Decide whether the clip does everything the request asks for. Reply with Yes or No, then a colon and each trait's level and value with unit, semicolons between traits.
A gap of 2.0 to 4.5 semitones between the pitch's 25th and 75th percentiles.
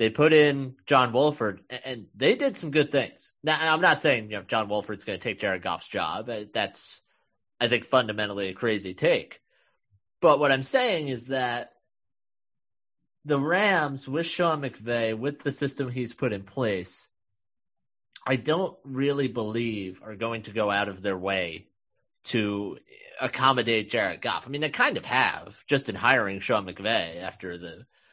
No: average, 5.1 semitones